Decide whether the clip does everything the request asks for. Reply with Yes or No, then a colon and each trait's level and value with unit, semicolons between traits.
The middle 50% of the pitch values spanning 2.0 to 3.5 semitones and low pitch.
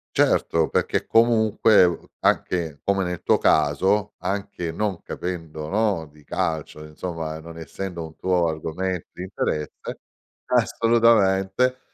No: average, 3.9 semitones; very low, 90 Hz